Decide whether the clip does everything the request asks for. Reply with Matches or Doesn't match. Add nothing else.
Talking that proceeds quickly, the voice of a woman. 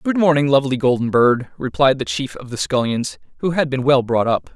Doesn't match